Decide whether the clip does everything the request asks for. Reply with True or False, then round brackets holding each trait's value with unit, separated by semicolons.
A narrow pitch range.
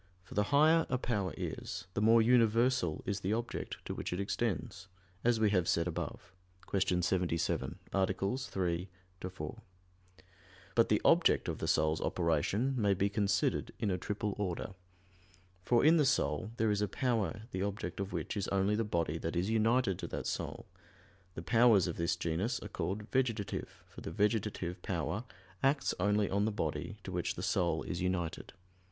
False (3.9 semitones)